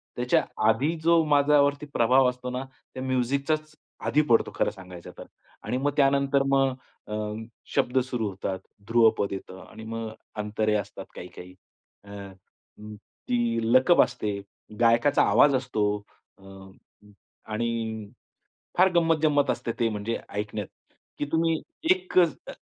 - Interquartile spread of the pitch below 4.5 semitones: No, average, 4.9 semitones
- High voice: No, low, 120 Hz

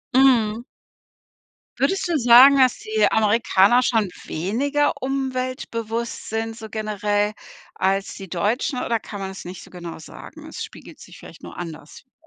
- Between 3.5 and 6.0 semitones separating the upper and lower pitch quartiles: Yes, average, 4.1 semitones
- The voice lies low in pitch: No, high, 225 Hz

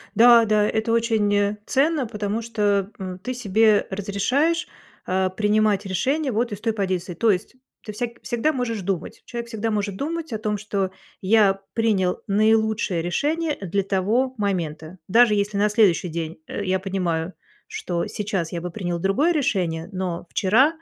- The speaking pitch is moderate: No, high, 210 Hz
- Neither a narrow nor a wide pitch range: Yes, average, 3.5 semitones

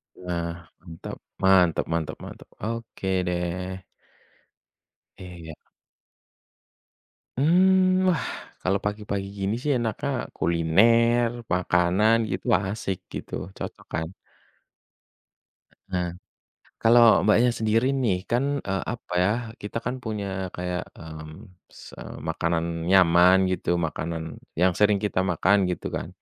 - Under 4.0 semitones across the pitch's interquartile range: No, average, 4.4 semitones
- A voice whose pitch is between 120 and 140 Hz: No, very low, 95 Hz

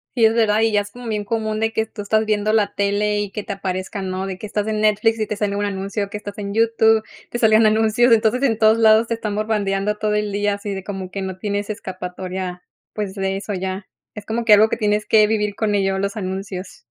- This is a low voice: No, high, 210 Hz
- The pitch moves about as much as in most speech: No, narrow, 1.7 semitones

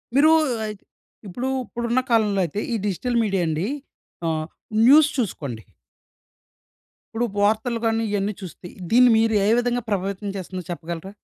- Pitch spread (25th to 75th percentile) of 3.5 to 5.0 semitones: Yes, average, 4.3 semitones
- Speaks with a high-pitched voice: Yes, high, 205 Hz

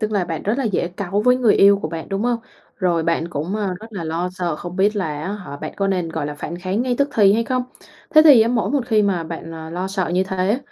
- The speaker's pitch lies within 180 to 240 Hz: Yes, high, 190 Hz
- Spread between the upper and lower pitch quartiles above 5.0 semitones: No, average, 4.2 semitones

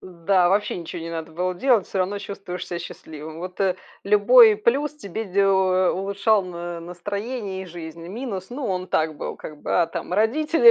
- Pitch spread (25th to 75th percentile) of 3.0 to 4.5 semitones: Yes, average, 3.3 semitones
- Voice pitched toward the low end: No, high, 190 Hz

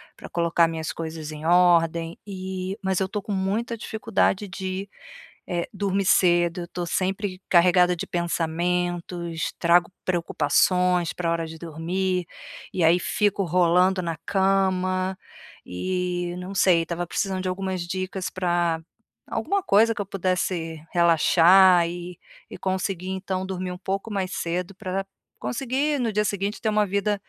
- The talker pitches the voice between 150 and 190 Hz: Yes, medium, 185 Hz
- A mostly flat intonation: Yes, narrow, 2.0 semitones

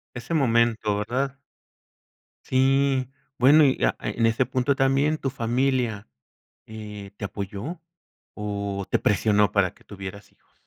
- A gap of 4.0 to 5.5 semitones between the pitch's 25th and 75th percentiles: Yes, average, 4.5 semitones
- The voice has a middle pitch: No, low, 115 Hz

